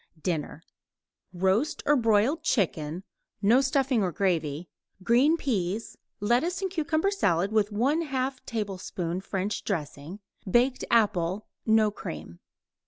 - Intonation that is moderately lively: No, wide, 6.5 semitones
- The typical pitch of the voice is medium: No, high, 210 Hz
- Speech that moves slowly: Yes, slow, 110 wpm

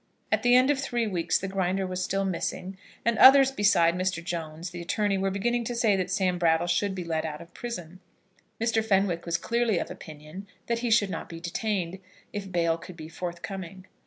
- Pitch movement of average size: Yes, average, 4.1 semitones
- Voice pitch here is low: No, high, 190 Hz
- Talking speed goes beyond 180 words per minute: Yes, fast, 205 wpm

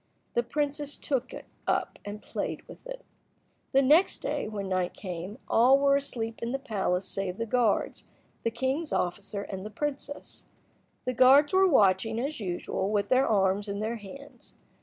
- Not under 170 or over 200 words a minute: Yes, average, 175 wpm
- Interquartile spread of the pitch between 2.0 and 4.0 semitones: No, wide, 5.6 semitones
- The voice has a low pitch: No, high, 230 Hz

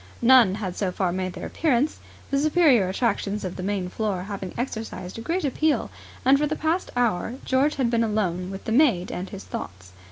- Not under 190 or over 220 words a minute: Yes, average, 200 wpm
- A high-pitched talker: Yes, high, 220 Hz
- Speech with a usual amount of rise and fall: No, wide, 6.2 semitones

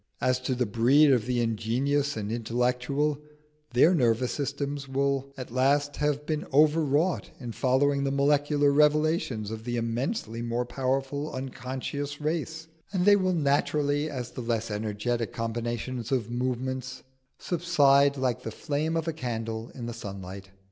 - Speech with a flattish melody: No, average, 3.5 semitones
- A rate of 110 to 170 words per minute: Yes, average, 150 wpm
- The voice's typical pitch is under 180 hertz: Yes, low, 135 Hz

